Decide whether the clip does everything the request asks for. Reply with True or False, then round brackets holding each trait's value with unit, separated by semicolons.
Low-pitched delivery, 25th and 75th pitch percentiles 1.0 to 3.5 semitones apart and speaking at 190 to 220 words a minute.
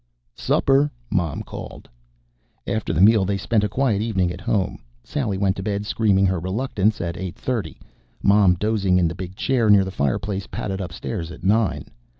False (100 Hz; 2.8 semitones; 175 wpm)